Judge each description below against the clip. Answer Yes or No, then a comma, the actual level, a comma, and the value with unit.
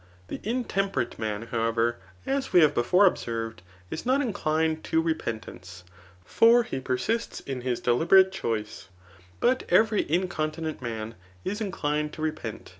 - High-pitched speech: No, medium, 155 Hz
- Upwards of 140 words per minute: No, slow, 135 wpm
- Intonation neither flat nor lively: No, wide, 8.8 semitones